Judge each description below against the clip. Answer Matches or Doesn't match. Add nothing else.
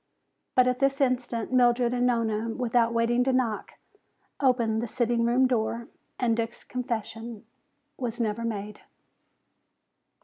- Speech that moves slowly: Matches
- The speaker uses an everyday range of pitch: Doesn't match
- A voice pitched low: Doesn't match